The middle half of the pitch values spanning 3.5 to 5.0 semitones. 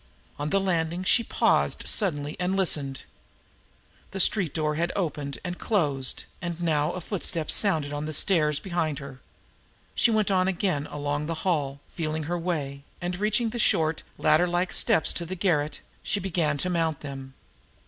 Yes: average, 3.9 semitones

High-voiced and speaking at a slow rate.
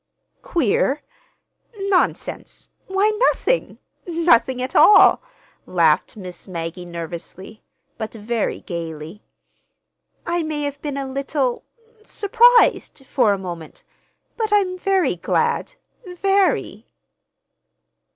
Yes: very high, 275 Hz; slow, 85 wpm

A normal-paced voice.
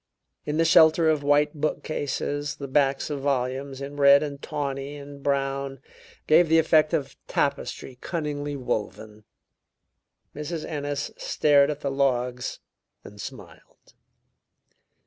No: slow, 125 wpm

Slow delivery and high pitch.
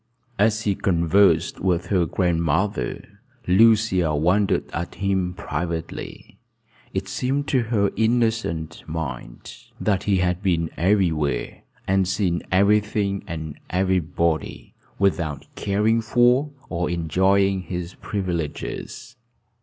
No: slow, 105 wpm; very low, 95 Hz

